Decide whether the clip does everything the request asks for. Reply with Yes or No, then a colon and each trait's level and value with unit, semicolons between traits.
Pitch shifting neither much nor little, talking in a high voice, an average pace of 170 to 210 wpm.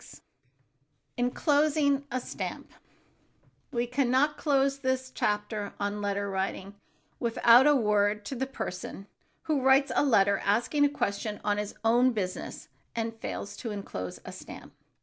No: average, 4.9 semitones; high, 235 Hz; average, 145 wpm